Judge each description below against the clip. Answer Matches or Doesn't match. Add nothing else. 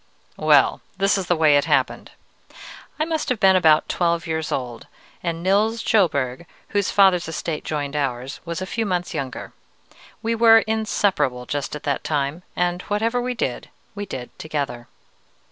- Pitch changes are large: Matches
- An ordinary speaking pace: Matches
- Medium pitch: Matches